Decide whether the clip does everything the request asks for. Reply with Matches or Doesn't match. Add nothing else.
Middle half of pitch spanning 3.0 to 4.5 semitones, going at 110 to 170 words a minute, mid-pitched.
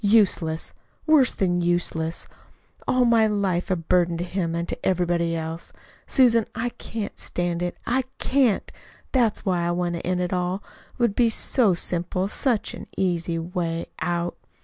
Matches